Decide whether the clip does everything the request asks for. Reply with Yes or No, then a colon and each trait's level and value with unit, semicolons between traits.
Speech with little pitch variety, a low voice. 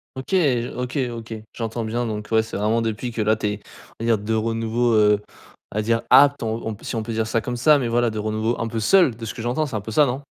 Yes: narrow, 1.8 semitones; low, 115 Hz